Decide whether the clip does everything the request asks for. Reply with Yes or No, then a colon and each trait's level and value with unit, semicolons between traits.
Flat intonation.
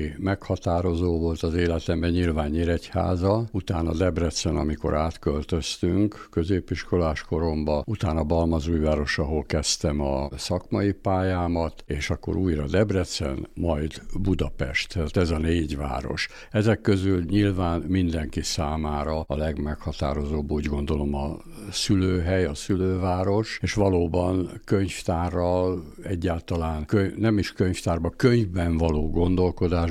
No: average, 3.3 semitones